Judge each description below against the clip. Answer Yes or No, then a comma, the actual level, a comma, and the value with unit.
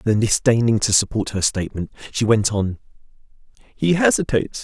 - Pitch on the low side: Yes, low, 115 Hz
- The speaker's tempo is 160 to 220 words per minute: No, average, 140 wpm